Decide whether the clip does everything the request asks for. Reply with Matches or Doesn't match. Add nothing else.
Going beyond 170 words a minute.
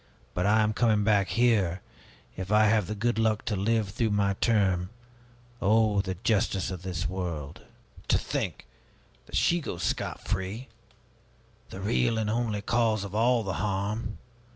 Doesn't match